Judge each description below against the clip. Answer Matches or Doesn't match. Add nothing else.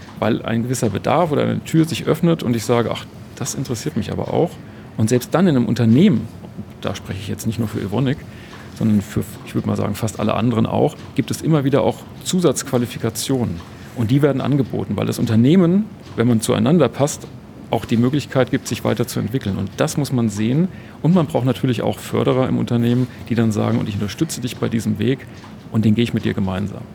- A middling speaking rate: Doesn't match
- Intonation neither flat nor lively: Matches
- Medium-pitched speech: Doesn't match